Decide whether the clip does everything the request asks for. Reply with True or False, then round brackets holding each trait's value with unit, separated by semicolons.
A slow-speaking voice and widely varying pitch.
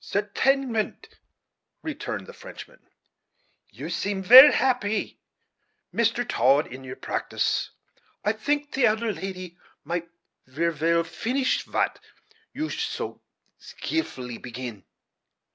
True (105 wpm; 7.8 semitones)